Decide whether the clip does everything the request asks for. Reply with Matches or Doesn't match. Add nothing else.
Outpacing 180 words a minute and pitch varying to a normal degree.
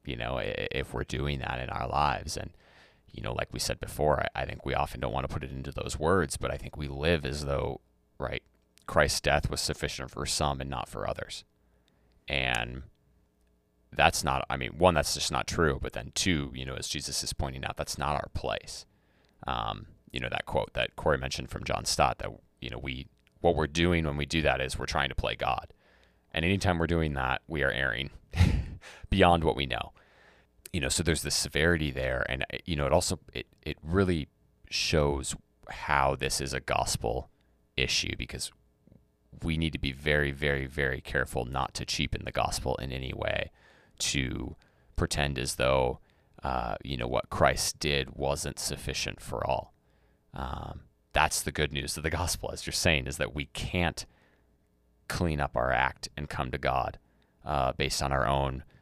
Matches